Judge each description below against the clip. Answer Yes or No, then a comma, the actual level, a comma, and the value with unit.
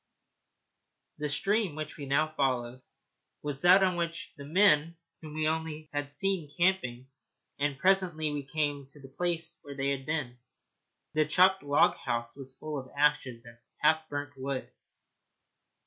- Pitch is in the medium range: Yes, medium, 150 Hz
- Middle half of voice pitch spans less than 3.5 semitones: Yes, average, 2.9 semitones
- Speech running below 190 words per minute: Yes, average, 160 wpm